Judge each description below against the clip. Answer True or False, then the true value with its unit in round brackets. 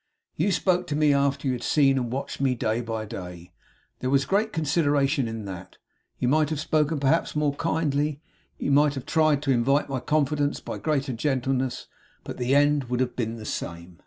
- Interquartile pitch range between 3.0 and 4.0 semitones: True (3.5 semitones)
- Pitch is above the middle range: False (140 Hz)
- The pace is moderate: True (195 wpm)